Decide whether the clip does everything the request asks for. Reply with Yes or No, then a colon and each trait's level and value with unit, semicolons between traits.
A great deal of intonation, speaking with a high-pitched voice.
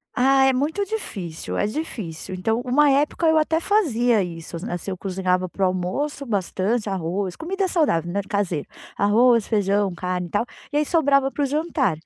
Yes: wide, 7.7 semitones; high, 220 Hz